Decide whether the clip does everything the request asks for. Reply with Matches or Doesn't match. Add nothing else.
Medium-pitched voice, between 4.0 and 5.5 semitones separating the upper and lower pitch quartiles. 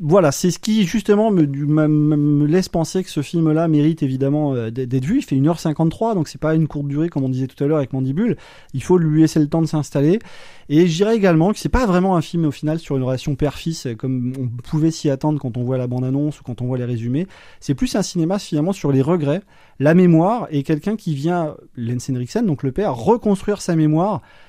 Matches